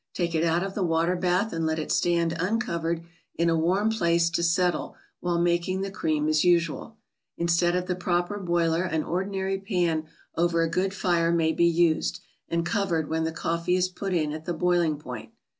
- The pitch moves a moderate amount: No, narrow, 1.8 semitones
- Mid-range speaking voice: Yes, medium, 170 Hz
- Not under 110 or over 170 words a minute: No, average, 195 wpm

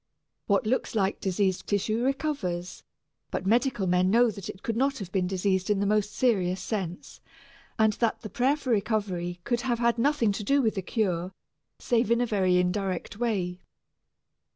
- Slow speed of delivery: No, average, 175 wpm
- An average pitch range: Yes, average, 4.1 semitones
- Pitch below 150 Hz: No, high, 210 Hz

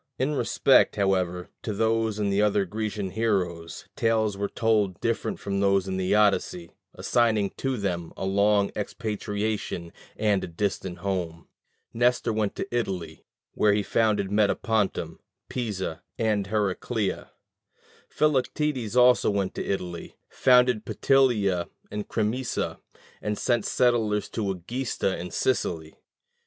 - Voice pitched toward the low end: Yes, low, 105 Hz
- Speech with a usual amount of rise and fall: Yes, average, 3.0 semitones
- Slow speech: Yes, slow, 125 wpm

